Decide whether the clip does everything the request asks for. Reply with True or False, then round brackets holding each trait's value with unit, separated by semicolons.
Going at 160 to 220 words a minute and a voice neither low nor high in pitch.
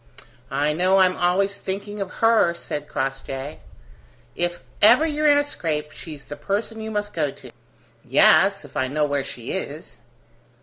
True (165 wpm; 175 Hz)